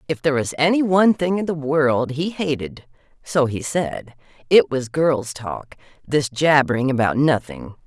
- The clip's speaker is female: Yes, female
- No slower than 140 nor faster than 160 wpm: Yes, average, 155 wpm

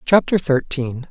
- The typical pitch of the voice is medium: Yes, medium, 150 Hz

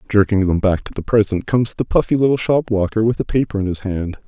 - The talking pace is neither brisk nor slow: No, fast, 255 wpm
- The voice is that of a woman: No, male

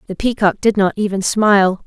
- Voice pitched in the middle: No, high, 200 Hz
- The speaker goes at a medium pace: Yes, average, 195 wpm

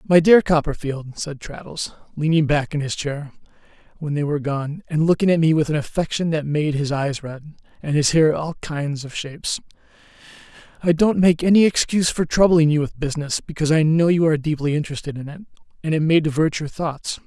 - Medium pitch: Yes, medium, 155 Hz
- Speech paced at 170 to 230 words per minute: Yes, average, 200 wpm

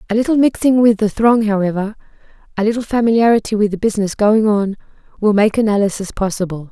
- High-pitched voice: Yes, high, 210 Hz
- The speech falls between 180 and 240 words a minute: No, average, 170 wpm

